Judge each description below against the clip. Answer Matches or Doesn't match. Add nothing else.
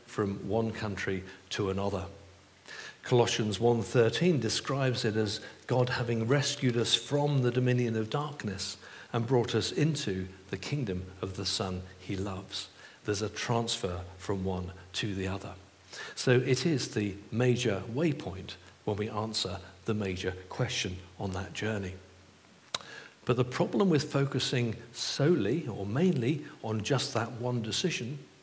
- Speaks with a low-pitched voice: Matches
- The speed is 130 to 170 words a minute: Matches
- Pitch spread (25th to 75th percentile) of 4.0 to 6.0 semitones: Matches